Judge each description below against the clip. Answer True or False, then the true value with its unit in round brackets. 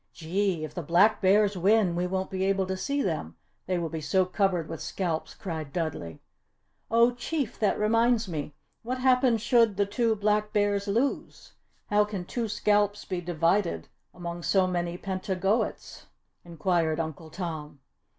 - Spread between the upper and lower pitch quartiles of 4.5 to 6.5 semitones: False (3.7 semitones)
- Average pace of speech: True (160 wpm)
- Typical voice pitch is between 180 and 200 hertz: True (190 Hz)